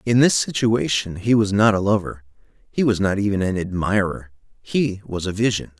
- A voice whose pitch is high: No, low, 100 Hz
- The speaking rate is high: No, average, 185 wpm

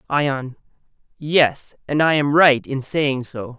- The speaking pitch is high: No, medium, 140 Hz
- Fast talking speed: No, average, 150 wpm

